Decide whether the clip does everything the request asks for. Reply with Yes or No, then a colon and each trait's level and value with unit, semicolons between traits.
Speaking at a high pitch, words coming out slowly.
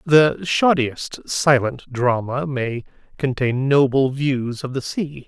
No: low, 135 Hz; slow, 125 wpm